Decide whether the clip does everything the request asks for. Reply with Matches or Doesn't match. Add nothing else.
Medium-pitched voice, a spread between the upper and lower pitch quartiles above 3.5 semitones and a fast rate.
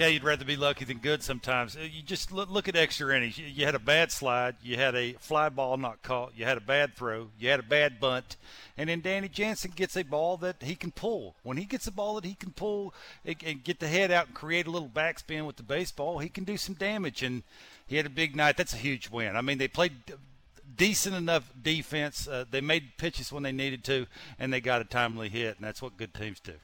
Matches